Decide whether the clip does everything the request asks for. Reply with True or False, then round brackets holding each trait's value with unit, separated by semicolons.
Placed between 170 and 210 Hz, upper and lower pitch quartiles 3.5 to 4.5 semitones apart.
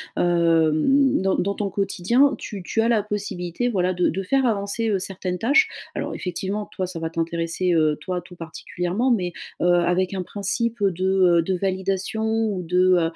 False (185 Hz; 2.7 semitones)